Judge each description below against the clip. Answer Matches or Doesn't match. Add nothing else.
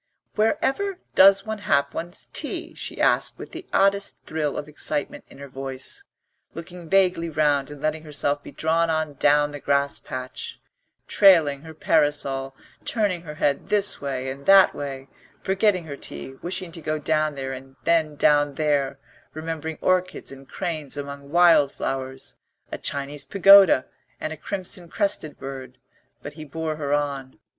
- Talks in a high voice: Doesn't match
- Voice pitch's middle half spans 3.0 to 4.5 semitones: Matches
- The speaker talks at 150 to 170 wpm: Matches